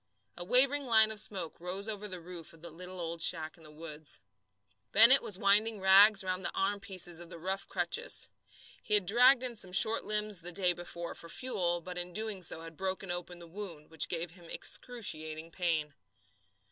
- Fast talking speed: No, average, 195 wpm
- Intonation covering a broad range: No, average, 3.8 semitones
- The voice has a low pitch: No, medium, 185 Hz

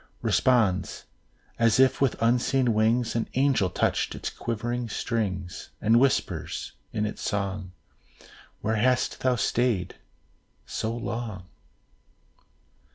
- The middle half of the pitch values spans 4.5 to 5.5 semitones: No, average, 3.2 semitones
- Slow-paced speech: Yes, slow, 105 wpm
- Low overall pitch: Yes, low, 115 Hz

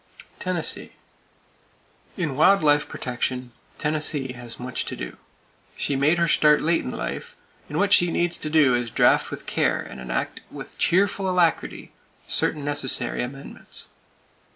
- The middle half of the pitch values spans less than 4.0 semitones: No, average, 5.2 semitones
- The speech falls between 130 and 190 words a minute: Yes, average, 150 wpm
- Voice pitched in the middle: Yes, medium, 150 Hz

